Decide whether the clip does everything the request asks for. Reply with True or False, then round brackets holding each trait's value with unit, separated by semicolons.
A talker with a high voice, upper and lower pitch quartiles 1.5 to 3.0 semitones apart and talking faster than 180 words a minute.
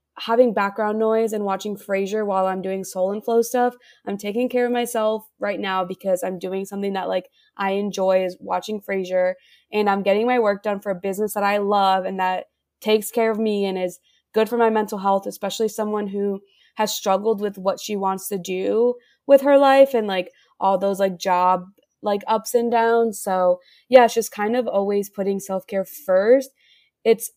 True (205 Hz; 2.7 semitones; 200 wpm)